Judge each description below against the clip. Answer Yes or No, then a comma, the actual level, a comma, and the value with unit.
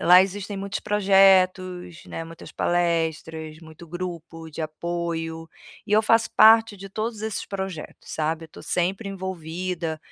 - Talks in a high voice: No, medium, 180 Hz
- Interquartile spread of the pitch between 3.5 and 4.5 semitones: No, average, 3.1 semitones